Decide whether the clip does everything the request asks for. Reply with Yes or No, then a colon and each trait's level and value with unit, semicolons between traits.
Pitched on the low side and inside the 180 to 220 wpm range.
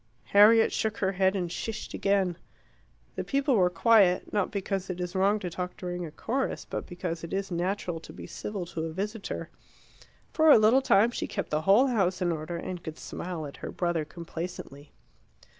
No: medium, 185 Hz; average, 190 wpm